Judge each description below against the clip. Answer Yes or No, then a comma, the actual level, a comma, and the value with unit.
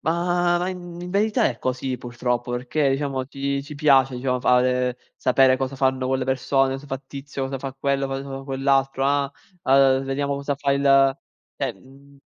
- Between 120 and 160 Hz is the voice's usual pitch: Yes, low, 135 Hz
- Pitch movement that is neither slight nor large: No, narrow, 1.1 semitones